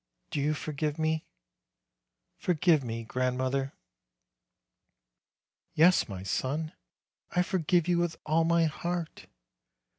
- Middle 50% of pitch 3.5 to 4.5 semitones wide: Yes, average, 3.9 semitones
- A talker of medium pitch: Yes, medium, 155 Hz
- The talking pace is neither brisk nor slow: No, slow, 110 wpm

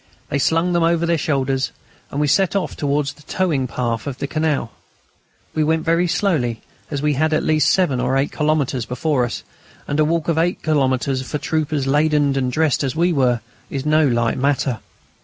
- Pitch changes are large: No, average, 3.2 semitones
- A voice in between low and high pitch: Yes, medium, 145 Hz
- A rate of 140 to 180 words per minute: No, average, 195 wpm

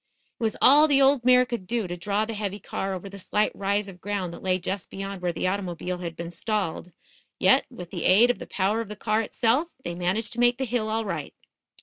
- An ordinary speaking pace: No, fast, 245 wpm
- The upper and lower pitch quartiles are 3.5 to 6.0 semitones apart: Yes, average, 3.9 semitones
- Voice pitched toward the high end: Yes, high, 200 Hz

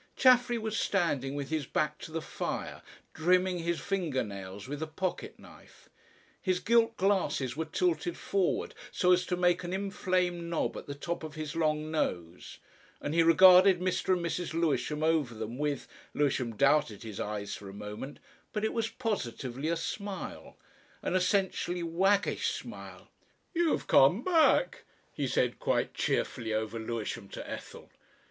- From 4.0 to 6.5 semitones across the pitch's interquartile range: Yes, wide, 5.4 semitones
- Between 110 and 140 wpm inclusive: No, average, 160 wpm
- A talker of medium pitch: Yes, medium, 165 Hz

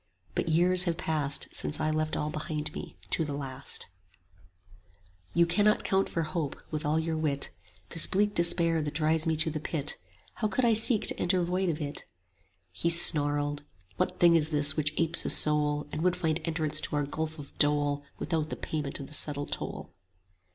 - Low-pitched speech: No, medium, 155 Hz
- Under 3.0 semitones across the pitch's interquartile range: Yes, narrow, 2.4 semitones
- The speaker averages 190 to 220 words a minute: Yes, average, 195 wpm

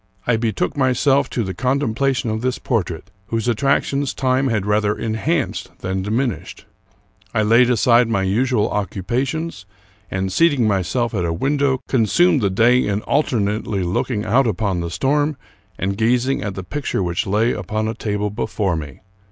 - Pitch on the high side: No, low, 115 Hz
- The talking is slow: No, average, 165 wpm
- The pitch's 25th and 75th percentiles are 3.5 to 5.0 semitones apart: Yes, average, 4.6 semitones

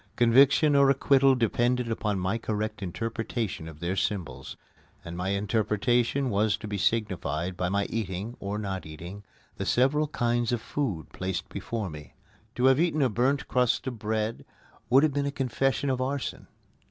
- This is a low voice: Yes, low, 115 Hz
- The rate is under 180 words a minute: Yes, average, 165 wpm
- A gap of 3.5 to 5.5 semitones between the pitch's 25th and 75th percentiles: Yes, average, 4.7 semitones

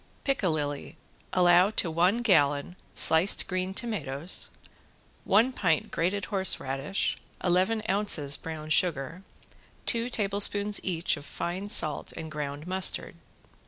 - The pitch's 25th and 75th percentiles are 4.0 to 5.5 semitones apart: Yes, average, 4.7 semitones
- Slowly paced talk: Yes, slow, 110 wpm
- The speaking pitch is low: No, medium, 180 Hz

